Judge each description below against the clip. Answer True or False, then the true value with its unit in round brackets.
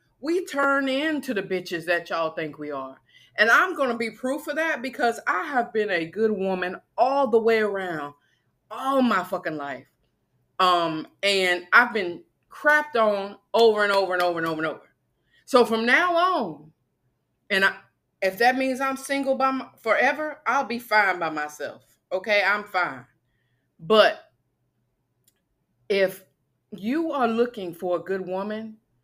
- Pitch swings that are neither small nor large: False (8.0 semitones)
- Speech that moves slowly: False (160 wpm)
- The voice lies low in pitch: False (200 Hz)